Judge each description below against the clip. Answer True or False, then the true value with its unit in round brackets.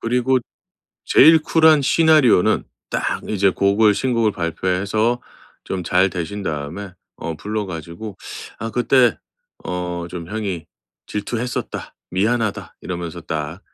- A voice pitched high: False (100 Hz)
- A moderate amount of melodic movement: True (5.0 semitones)